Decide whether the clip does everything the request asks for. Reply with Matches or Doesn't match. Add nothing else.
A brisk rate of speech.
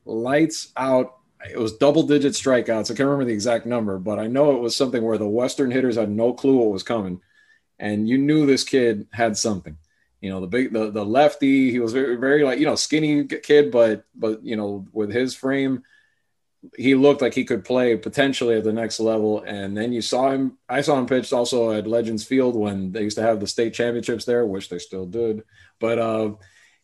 Matches